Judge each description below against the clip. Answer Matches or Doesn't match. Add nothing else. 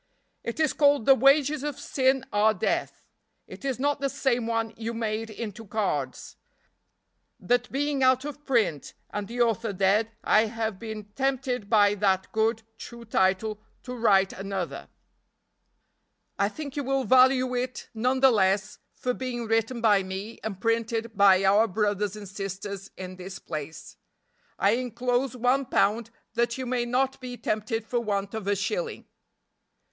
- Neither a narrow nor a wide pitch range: Matches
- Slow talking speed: Doesn't match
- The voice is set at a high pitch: Matches